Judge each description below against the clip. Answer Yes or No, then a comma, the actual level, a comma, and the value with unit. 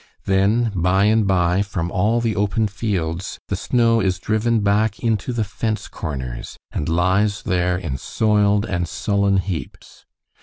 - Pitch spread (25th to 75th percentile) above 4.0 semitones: No, average, 3.2 semitones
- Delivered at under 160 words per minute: Yes, average, 150 wpm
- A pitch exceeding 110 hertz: No, low, 100 Hz